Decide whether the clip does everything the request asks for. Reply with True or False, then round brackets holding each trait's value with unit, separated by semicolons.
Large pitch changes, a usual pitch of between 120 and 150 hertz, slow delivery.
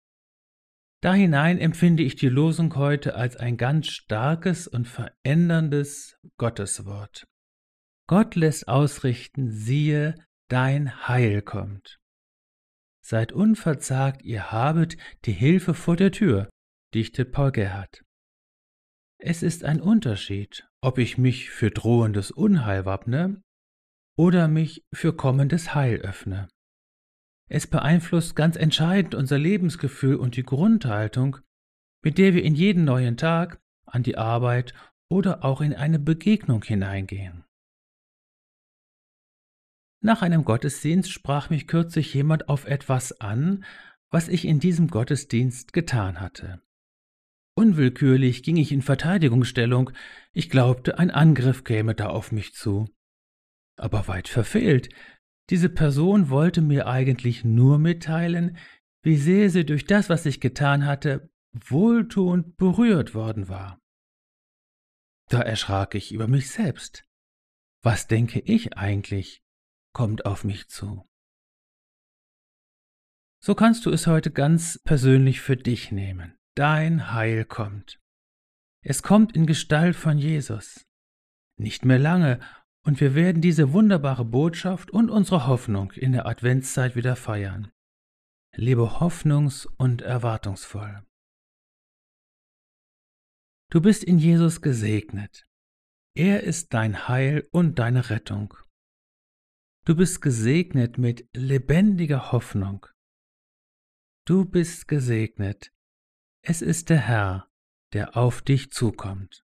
True (6.7 semitones; 135 Hz; 115 wpm)